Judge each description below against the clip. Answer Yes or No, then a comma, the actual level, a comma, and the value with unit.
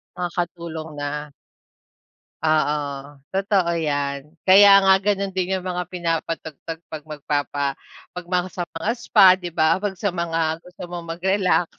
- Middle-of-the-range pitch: Yes, medium, 170 Hz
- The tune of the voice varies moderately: Yes, average, 3.0 semitones